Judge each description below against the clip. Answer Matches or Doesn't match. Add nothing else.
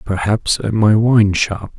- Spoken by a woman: Doesn't match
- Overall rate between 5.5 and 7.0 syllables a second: Doesn't match